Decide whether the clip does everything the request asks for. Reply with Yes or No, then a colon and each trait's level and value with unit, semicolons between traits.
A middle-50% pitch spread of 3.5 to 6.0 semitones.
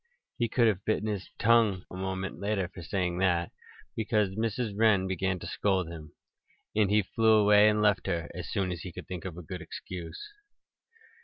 No: average, 2.9 semitones